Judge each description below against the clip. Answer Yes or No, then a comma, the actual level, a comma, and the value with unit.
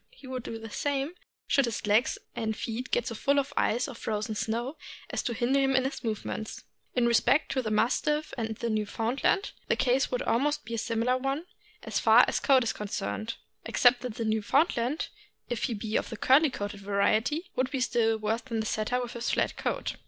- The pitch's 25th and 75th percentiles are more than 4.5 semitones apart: No, average, 3.4 semitones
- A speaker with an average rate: No, fast, 210 wpm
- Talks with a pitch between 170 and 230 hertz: No, high, 240 Hz